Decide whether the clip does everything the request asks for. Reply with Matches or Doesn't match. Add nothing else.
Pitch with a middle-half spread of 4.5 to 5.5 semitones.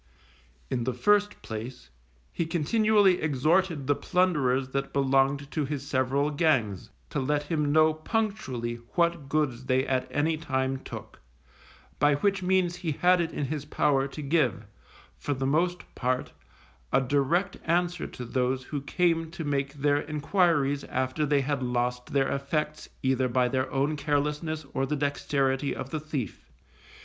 Doesn't match